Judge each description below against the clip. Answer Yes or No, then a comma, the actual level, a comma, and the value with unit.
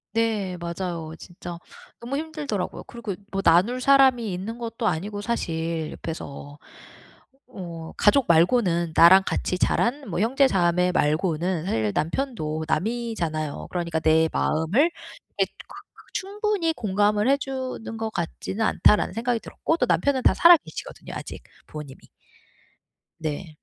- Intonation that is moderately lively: No, wide, 6.4 semitones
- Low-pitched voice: No, high, 195 Hz